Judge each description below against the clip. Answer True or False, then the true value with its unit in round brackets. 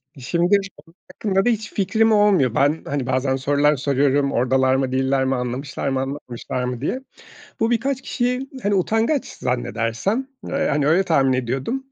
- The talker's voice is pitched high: False (145 Hz)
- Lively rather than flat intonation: True (7.9 semitones)